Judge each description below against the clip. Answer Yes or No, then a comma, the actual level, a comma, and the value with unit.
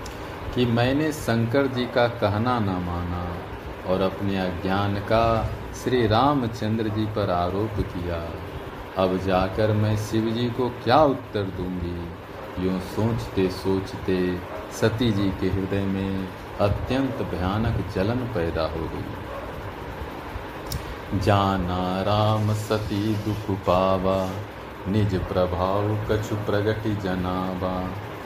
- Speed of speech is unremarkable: No, slow, 105 wpm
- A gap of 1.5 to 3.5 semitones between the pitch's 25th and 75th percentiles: Yes, narrow, 2.6 semitones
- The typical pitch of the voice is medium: No, low, 100 Hz